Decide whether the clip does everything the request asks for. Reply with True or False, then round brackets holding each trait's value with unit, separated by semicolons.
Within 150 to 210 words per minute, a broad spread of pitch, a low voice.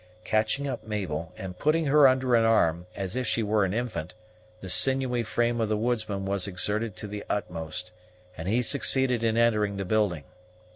False (185 wpm; 4.0 semitones; 110 Hz)